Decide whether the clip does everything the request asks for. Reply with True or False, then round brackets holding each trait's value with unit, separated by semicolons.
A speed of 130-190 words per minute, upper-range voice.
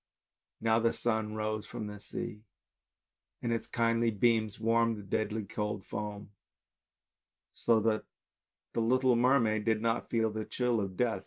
False (155 wpm; 110 Hz)